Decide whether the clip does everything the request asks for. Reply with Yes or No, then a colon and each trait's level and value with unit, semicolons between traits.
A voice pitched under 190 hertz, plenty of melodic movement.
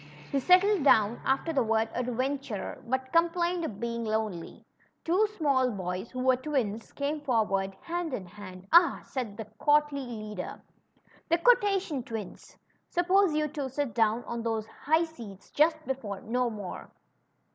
No: very high, 255 Hz; wide, 6.0 semitones